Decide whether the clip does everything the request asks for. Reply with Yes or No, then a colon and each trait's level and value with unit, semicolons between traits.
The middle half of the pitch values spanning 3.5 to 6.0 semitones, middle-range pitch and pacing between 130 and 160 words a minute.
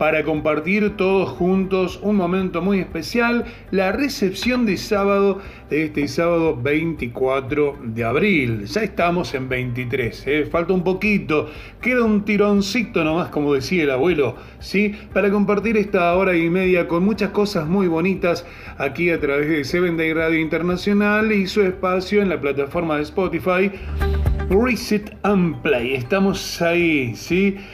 Yes: average, 4.4 semitones; medium, 180 Hz; average, 145 wpm